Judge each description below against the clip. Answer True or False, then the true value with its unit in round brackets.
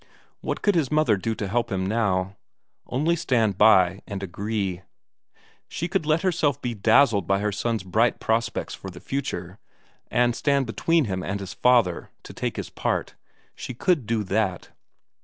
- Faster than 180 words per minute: False (175 wpm)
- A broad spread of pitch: False (5.0 semitones)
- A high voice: False (110 Hz)